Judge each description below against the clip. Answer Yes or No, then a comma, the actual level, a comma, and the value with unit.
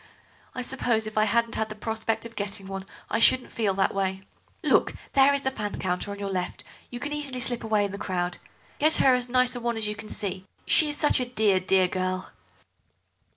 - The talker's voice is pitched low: No, high, 220 Hz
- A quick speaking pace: Yes, fast, 220 wpm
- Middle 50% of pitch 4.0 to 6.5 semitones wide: Yes, average, 4.3 semitones